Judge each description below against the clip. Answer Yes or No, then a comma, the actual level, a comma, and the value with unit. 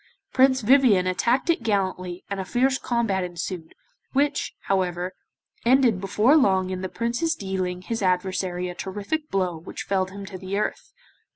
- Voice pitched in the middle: No, high, 195 Hz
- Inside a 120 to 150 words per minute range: No, average, 160 wpm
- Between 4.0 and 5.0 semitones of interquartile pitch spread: Yes, average, 4.4 semitones